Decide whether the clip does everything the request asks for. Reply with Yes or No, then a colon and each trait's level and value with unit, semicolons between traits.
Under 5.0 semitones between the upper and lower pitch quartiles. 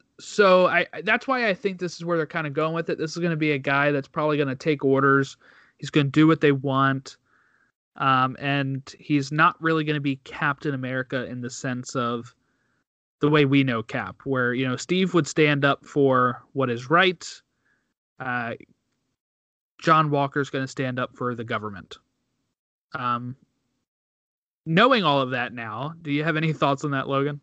Yes: average, 3.3 semitones